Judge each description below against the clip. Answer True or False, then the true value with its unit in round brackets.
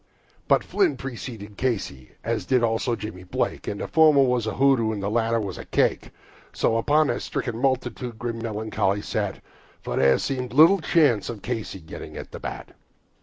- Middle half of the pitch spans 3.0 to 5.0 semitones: True (3.7 semitones)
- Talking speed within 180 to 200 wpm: True (185 wpm)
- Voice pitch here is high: False (115 Hz)